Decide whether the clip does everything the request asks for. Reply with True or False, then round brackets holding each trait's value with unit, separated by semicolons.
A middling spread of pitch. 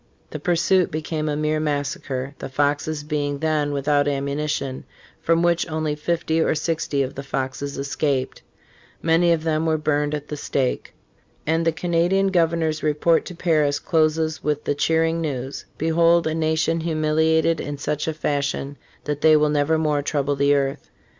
False (2.1 semitones)